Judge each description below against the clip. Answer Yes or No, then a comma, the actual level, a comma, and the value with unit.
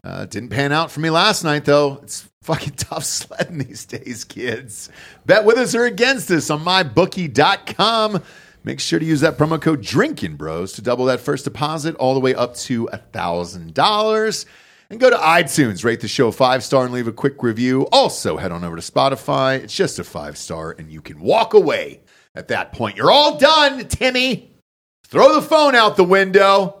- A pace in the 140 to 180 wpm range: No, average, 190 wpm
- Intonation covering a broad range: Yes, wide, 8.1 semitones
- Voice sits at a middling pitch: Yes, medium, 150 Hz